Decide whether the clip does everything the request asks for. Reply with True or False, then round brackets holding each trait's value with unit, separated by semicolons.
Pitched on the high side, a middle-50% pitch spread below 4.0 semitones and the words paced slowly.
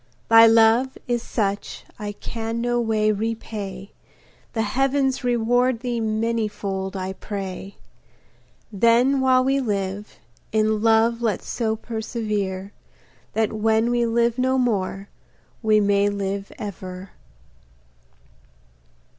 True (220 Hz; 2.8 semitones; 110 wpm)